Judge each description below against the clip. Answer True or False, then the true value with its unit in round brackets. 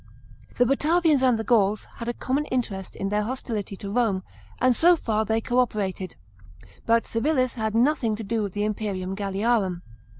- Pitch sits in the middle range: False (225 Hz)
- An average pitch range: True (3.7 semitones)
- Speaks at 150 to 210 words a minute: True (180 wpm)